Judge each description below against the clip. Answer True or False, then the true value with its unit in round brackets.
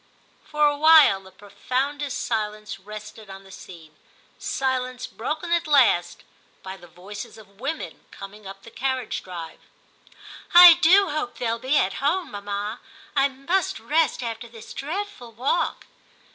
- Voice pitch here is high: True (245 Hz)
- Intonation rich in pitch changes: True (6.5 semitones)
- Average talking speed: True (150 wpm)